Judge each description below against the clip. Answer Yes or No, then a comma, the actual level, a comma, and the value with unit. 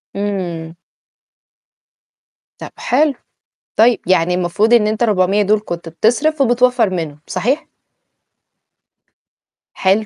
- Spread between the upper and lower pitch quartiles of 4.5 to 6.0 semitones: Yes, average, 5.0 semitones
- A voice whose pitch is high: Yes, high, 210 Hz